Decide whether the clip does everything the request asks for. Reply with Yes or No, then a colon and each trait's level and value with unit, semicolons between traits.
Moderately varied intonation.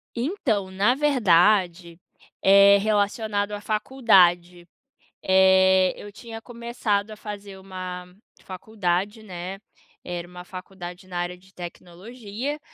Yes: average, 3.1 semitones